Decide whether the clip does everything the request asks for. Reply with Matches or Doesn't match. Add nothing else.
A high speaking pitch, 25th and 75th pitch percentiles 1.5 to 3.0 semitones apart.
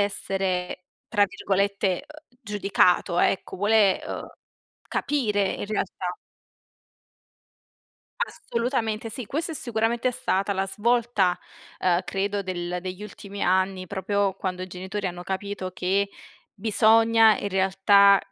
Matches